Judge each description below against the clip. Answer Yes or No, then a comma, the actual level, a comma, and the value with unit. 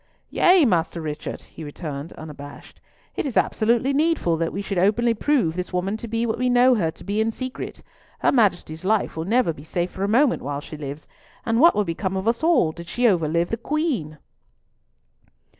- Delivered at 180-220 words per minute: Yes, average, 200 wpm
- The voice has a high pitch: Yes, high, 200 Hz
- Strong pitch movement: Yes, wide, 6.6 semitones